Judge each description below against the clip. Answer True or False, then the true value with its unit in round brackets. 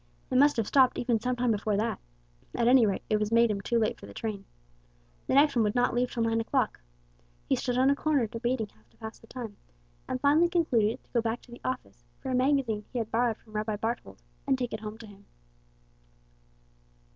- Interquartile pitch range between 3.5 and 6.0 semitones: False (2.9 semitones)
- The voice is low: False (230 Hz)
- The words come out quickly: True (230 wpm)